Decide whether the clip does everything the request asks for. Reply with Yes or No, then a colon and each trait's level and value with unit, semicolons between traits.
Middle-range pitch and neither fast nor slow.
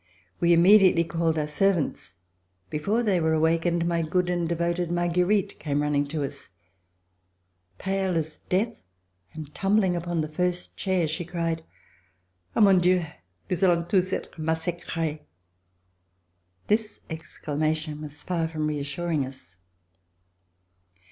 No: medium, 170 Hz; slow, 125 wpm